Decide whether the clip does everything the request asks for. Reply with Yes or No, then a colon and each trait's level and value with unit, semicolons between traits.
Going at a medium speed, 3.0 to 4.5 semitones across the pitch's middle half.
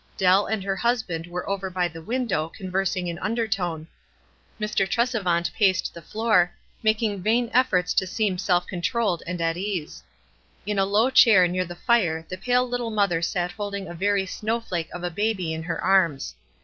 Yes: average, 180 wpm; average, 3.6 semitones